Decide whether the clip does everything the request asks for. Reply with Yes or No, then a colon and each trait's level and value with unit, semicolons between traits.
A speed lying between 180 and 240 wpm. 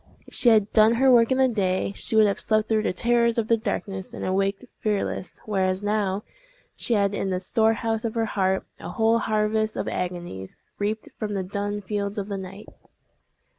Yes: average, 200 wpm